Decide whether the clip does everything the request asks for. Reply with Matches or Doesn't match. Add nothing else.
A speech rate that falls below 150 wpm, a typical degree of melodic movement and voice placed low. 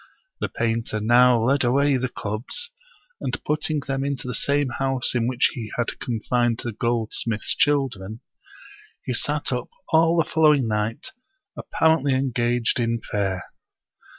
Matches